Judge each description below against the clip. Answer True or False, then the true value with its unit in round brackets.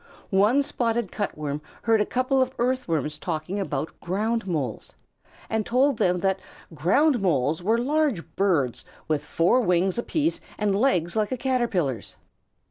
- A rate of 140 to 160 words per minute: True (145 wpm)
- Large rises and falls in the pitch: True (6.6 semitones)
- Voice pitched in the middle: False (200 Hz)